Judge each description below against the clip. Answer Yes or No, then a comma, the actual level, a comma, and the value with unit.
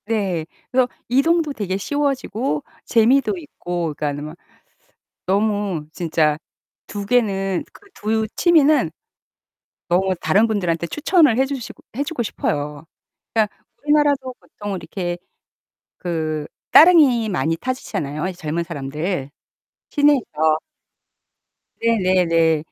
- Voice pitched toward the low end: No, high, 200 Hz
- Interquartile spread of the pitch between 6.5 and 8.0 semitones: Yes, wide, 7.7 semitones